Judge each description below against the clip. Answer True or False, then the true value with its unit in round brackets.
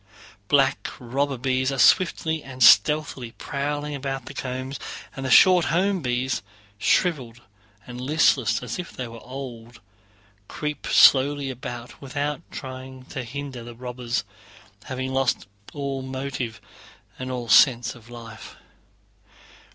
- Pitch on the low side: True (130 Hz)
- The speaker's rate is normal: False (130 wpm)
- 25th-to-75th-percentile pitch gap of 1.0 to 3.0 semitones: True (2.5 semitones)